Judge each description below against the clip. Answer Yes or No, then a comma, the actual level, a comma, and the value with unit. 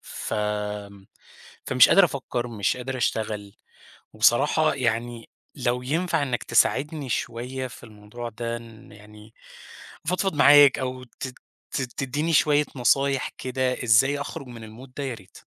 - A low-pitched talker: Yes, low, 125 Hz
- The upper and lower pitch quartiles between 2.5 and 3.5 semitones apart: Yes, average, 3.1 semitones